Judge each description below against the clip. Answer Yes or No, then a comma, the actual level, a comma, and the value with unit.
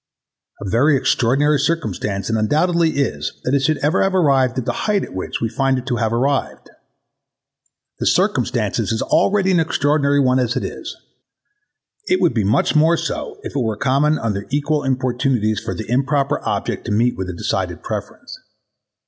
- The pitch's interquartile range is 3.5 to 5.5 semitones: Yes, average, 4.6 semitones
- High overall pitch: No, low, 135 Hz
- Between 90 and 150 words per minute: No, average, 180 wpm